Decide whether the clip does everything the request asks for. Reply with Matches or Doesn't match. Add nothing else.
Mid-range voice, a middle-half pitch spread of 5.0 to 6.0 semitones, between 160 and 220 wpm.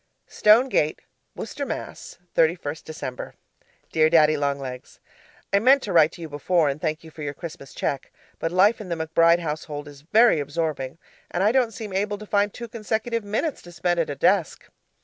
Matches